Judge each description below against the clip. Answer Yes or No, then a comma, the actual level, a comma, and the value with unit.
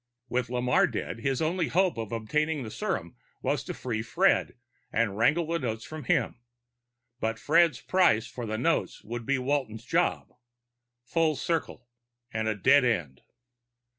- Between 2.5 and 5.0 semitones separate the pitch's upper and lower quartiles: No, wide, 5.6 semitones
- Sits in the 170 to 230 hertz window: No, low, 125 Hz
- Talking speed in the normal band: Yes, average, 155 wpm